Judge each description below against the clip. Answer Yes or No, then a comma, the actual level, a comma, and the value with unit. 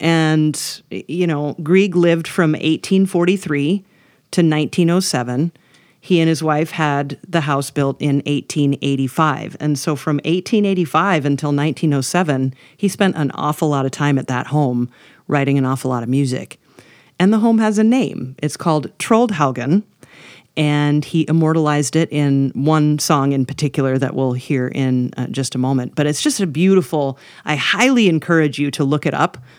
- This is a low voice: No, medium, 150 Hz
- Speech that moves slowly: No, average, 160 wpm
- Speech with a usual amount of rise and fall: Yes, average, 3.6 semitones